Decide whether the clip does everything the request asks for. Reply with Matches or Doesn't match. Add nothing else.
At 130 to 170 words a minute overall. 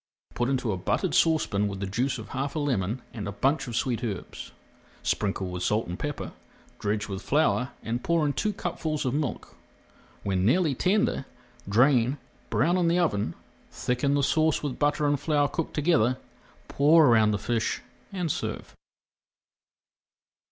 Matches